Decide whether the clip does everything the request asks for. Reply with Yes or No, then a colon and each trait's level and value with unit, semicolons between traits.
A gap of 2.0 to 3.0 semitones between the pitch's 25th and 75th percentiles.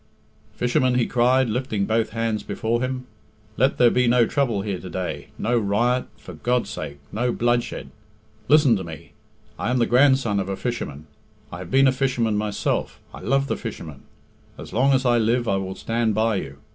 No: average, 3.5 semitones